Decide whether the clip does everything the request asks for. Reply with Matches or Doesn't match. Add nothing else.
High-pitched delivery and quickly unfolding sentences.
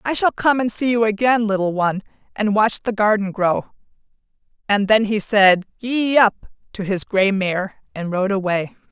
Doesn't match